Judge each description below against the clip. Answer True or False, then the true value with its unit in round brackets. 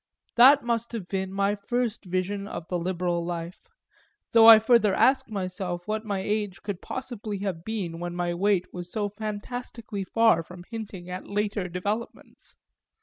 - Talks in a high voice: True (200 Hz)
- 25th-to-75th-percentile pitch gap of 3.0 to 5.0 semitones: True (3.5 semitones)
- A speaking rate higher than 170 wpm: False (160 wpm)